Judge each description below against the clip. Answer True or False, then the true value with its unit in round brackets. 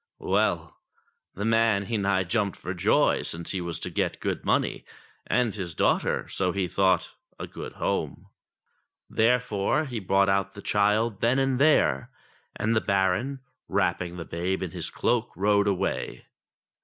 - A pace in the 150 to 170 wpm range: True (155 wpm)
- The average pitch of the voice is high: False (100 Hz)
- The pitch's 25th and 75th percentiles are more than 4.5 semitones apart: False (3.5 semitones)